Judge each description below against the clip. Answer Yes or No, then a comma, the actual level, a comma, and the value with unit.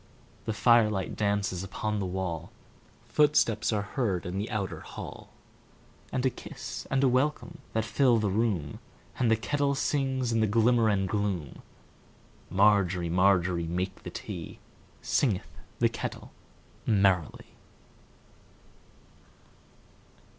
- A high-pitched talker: No, low, 105 Hz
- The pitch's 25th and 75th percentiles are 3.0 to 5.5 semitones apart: Yes, average, 4.0 semitones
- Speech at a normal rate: No, slow, 105 wpm